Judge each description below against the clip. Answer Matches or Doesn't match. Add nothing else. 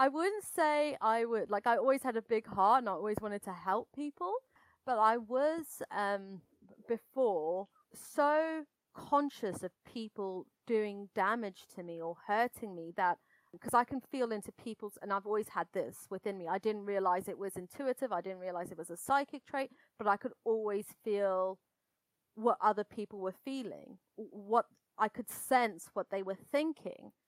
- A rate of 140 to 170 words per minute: Doesn't match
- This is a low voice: Doesn't match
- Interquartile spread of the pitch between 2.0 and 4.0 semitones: Doesn't match